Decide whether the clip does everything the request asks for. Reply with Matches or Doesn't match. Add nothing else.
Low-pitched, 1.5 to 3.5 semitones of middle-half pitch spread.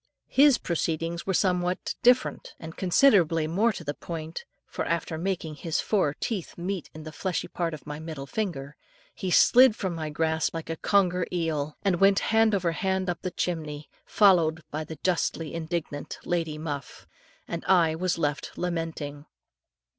Doesn't match